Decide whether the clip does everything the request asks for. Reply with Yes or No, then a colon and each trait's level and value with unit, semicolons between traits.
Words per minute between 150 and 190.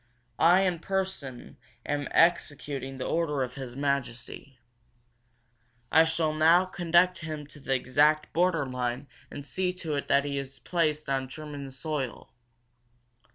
No: average, 140 wpm